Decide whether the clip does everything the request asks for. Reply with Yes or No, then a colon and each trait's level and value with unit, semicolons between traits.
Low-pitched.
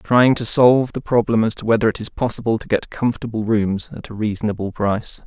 Yes: low, 110 Hz